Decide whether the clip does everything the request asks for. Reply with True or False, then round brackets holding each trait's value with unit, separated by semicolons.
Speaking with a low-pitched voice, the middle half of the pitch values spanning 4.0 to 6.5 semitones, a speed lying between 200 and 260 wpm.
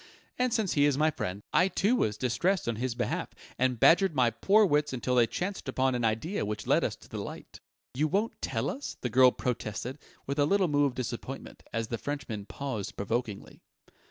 True (130 Hz; 5.2 semitones; 205 wpm)